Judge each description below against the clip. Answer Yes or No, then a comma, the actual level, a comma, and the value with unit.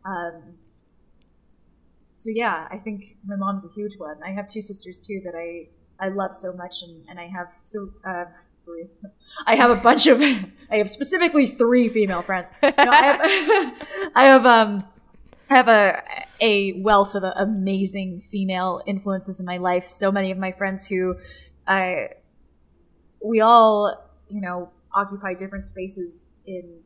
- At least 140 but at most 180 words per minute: Yes, average, 165 wpm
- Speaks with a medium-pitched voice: No, high, 195 Hz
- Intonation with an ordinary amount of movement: Yes, average, 3.3 semitones